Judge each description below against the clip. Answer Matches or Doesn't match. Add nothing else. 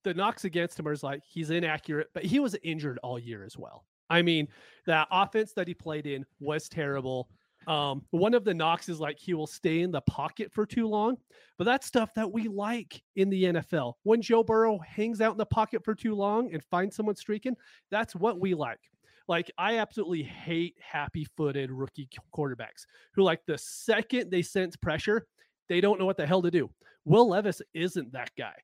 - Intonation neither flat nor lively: Doesn't match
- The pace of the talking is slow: Doesn't match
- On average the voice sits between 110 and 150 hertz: Doesn't match